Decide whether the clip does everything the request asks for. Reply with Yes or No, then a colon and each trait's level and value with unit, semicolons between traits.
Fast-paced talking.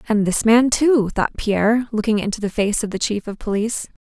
Yes: fast, 225 wpm